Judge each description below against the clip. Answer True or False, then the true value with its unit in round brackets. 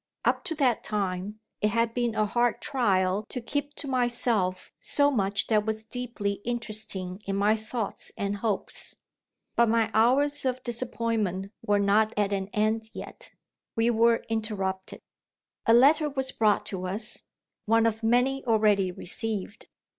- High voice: True (220 Hz)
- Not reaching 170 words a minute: True (150 wpm)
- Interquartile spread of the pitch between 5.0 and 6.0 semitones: False (3.1 semitones)